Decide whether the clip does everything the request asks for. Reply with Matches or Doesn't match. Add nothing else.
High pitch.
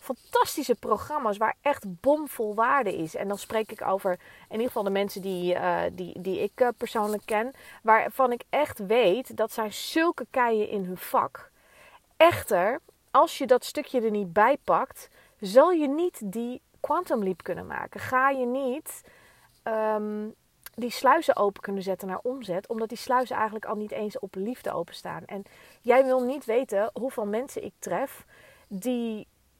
Matches